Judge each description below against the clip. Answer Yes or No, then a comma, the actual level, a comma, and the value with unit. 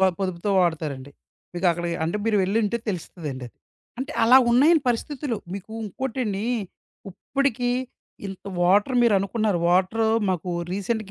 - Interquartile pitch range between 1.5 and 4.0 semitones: No, average, 4.9 semitones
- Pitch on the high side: Yes, high, 200 Hz